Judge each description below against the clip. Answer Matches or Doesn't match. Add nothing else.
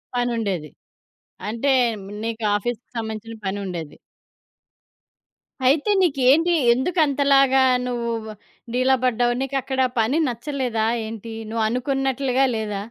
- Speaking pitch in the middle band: Doesn't match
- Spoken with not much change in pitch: Doesn't match